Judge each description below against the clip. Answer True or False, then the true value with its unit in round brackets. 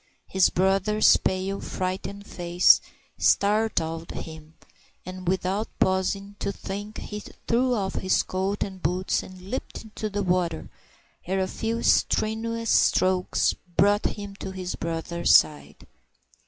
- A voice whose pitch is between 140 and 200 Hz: True (190 Hz)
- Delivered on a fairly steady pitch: True (2.1 semitones)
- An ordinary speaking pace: False (125 wpm)